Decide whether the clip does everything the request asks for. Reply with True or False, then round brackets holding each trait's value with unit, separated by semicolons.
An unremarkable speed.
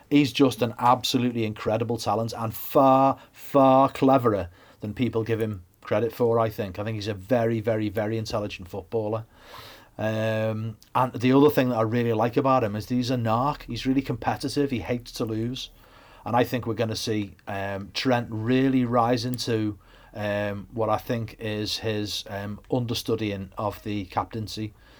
True (175 wpm)